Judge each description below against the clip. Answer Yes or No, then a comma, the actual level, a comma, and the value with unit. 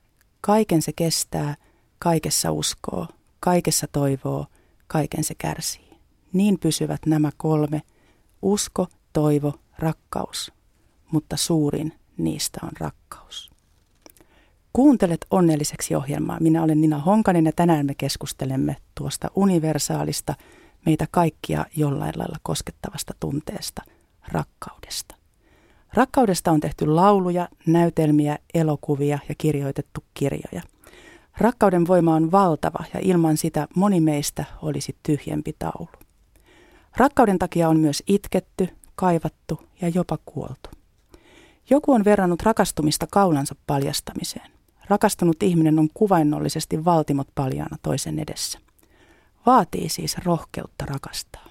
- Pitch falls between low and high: Yes, medium, 160 Hz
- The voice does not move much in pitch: No, average, 3.4 semitones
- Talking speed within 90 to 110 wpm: Yes, average, 105 wpm